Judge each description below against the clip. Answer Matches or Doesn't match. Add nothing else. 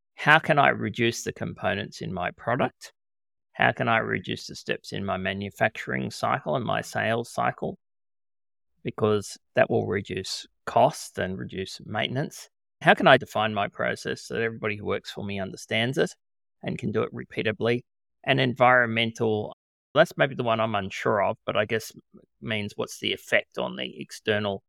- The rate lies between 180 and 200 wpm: Doesn't match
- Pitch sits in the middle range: Doesn't match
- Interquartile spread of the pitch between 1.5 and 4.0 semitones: Matches